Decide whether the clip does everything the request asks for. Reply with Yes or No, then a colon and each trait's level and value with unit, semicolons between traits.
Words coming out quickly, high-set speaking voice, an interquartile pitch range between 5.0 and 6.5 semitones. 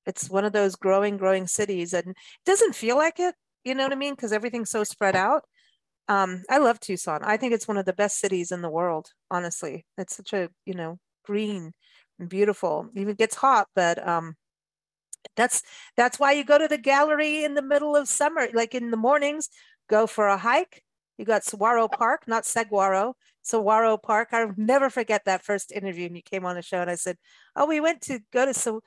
Yes: fast, 215 wpm; high, 215 Hz; wide, 5.5 semitones